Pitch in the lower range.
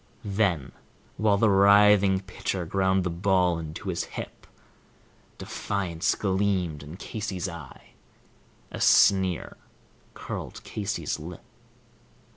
Yes: very low, 95 Hz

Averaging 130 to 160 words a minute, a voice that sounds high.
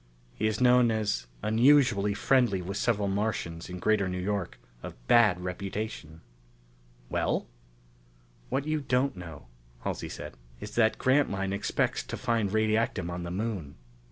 No: average, 140 wpm; low, 105 Hz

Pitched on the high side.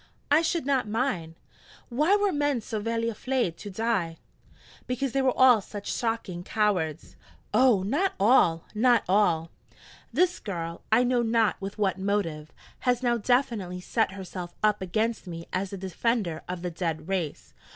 Yes: high, 210 Hz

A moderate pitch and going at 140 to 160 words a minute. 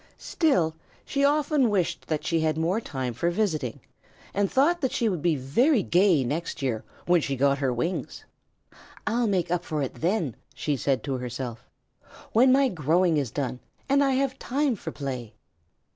No: medium, 170 Hz; average, 175 wpm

